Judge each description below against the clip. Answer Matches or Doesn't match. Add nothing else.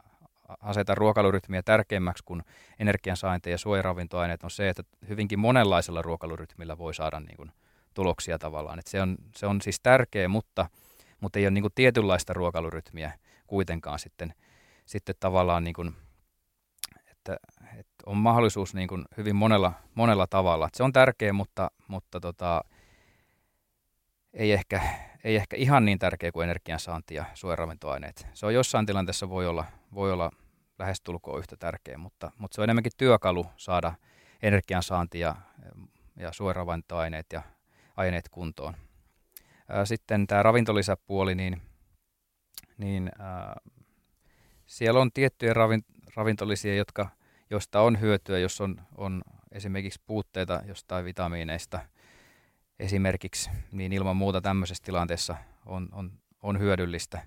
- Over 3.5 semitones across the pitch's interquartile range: Doesn't match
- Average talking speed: Matches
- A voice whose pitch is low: Matches